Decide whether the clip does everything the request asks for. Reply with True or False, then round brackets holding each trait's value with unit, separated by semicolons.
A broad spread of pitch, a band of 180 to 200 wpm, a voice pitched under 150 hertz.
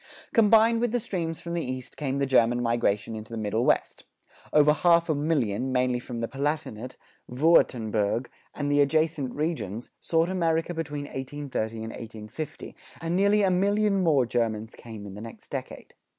False (6.1 semitones; 165 wpm; 140 Hz)